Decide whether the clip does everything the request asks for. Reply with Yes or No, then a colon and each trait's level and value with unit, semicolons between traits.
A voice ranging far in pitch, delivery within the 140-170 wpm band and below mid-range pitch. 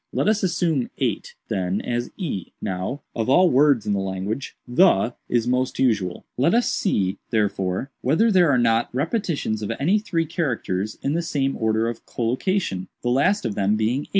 No: wide, 7.4 semitones; average, 180 wpm; low, 125 Hz